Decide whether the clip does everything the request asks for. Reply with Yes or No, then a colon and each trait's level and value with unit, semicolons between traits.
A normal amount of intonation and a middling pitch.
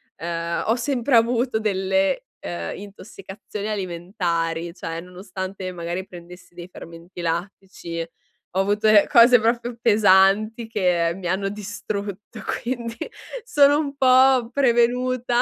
No: average, 4.6 semitones; high, 200 Hz